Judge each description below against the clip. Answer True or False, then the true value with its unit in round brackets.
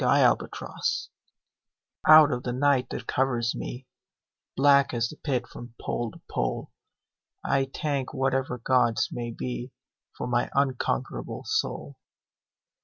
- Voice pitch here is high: False (130 Hz)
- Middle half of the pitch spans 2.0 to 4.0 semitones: True (2.4 semitones)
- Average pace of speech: False (130 wpm)